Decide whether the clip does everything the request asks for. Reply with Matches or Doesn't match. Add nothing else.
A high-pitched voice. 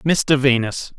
Doesn't match